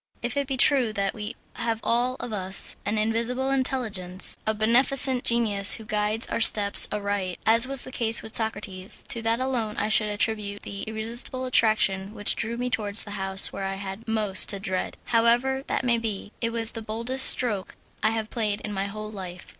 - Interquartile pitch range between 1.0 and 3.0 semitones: Yes, narrow, 2.6 semitones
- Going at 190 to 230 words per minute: Yes, average, 195 wpm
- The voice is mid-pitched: No, high, 220 Hz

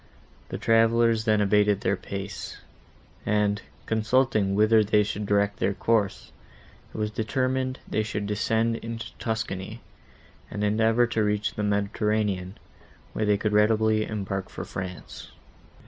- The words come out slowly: Yes, slow, 130 wpm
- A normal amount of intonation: No, narrow, 1.6 semitones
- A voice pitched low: Yes, low, 105 Hz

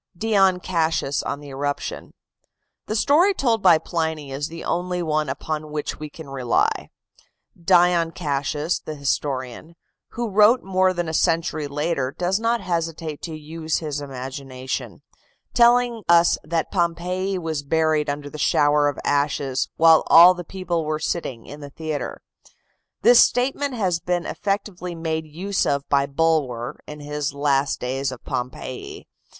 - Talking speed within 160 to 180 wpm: No, average, 145 wpm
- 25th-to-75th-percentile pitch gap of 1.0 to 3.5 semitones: No, average, 3.9 semitones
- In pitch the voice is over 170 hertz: No, medium, 160 Hz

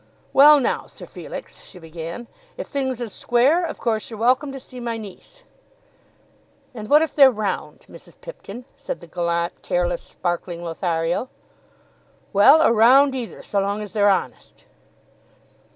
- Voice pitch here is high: Yes, high, 230 Hz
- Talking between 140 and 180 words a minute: Yes, average, 150 wpm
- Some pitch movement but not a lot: No, wide, 6.1 semitones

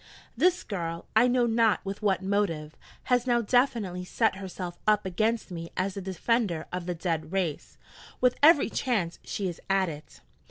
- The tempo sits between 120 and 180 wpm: Yes, average, 170 wpm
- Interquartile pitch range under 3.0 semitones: No, average, 4.9 semitones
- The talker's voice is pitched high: Yes, high, 195 Hz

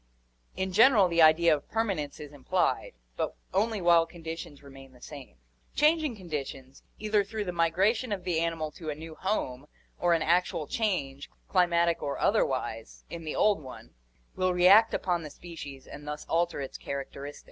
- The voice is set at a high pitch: No, medium, 170 Hz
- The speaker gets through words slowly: No, average, 170 wpm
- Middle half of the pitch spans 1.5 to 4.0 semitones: No, average, 4.5 semitones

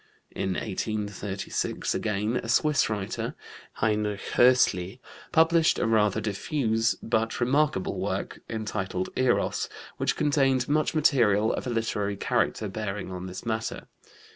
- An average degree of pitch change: Yes, average, 3.7 semitones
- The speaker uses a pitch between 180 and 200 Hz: No, low, 110 Hz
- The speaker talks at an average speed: No, slow, 120 wpm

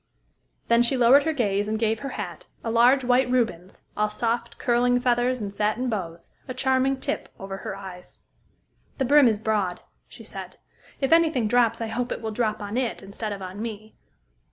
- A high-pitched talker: Yes, high, 230 Hz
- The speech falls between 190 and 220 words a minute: Yes, average, 195 wpm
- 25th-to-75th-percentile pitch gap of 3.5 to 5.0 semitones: No, average, 3.0 semitones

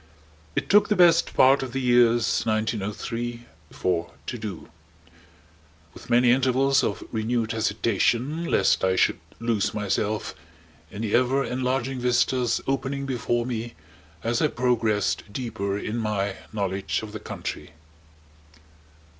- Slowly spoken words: Yes, slow, 130 wpm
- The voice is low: Yes, low, 120 Hz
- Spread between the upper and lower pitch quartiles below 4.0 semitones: Yes, average, 3.1 semitones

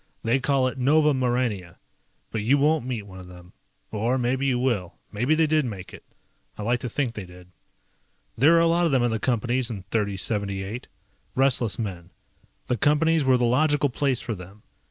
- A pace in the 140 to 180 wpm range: No, average, 195 wpm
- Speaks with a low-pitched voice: Yes, low, 120 Hz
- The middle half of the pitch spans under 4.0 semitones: No, average, 4.9 semitones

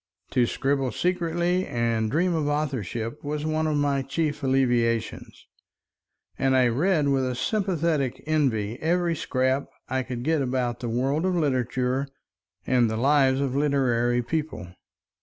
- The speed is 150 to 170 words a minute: No, average, 140 wpm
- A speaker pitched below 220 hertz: Yes, low, 135 Hz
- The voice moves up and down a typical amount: Yes, average, 4.0 semitones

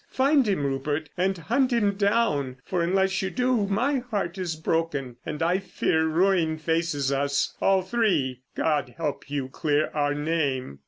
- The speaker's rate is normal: Yes, average, 155 wpm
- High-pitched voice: No, medium, 165 Hz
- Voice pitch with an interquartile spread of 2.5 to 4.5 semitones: No, average, 5.1 semitones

